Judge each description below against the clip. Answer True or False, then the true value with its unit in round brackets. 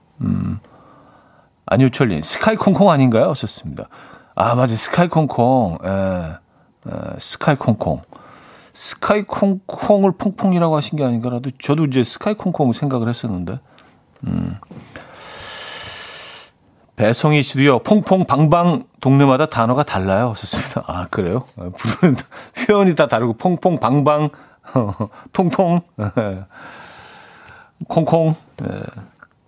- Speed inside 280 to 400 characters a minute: False (235 characters per minute)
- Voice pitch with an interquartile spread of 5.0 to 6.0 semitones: False (6.8 semitones)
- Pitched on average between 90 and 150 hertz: True (140 Hz)